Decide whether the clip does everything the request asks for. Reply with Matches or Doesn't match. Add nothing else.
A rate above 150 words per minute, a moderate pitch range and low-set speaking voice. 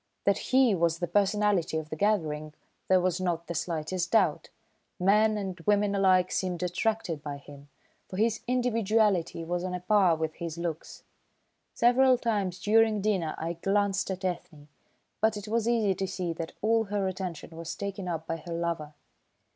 Doesn't match